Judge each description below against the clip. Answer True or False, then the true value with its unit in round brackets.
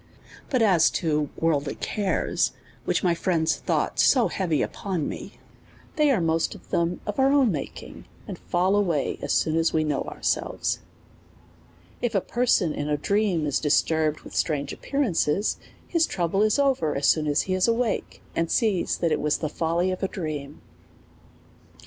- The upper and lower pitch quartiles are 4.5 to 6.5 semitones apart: True (5.1 semitones)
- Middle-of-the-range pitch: True (170 Hz)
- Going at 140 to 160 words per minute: False (175 wpm)